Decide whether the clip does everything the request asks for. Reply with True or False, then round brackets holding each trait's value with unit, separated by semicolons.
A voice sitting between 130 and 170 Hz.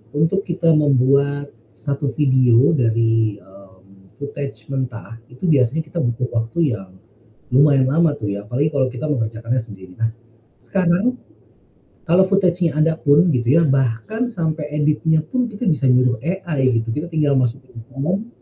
True (140 Hz)